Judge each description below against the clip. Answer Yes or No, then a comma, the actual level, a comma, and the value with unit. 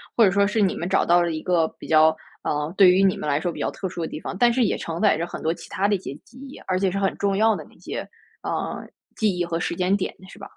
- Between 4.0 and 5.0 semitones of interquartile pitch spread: No, average, 3.0 semitones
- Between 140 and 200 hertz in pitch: Yes, medium, 185 Hz